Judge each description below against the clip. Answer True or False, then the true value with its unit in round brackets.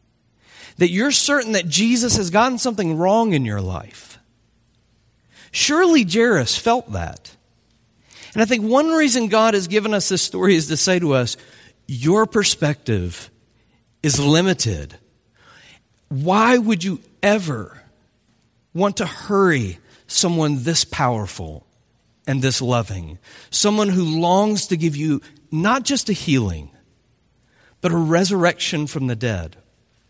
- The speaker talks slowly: True (130 wpm)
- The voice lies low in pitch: False (155 Hz)